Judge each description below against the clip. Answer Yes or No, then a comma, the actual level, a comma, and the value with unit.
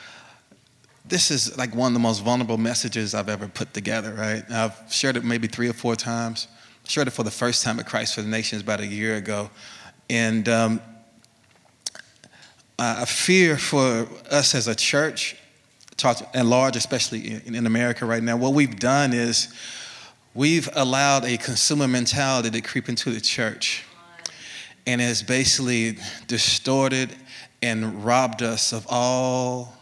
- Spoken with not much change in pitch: Yes, narrow, 2.2 semitones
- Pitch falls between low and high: No, low, 120 Hz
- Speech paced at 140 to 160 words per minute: Yes, average, 155 wpm